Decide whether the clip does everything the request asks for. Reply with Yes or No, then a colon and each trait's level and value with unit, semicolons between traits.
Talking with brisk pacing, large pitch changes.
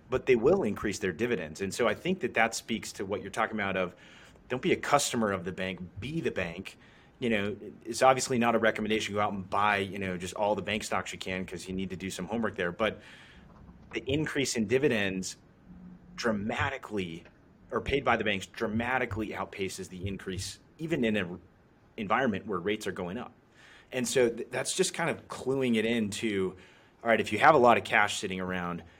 No: fast, 215 wpm; average, 3.9 semitones